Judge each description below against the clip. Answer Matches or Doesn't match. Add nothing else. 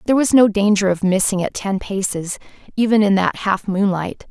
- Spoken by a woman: Matches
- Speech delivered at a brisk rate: Doesn't match